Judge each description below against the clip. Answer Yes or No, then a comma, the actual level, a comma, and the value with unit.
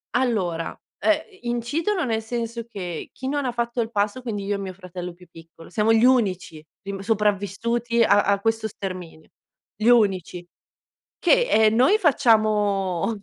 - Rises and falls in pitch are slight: No, average, 3.6 semitones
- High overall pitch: Yes, high, 215 Hz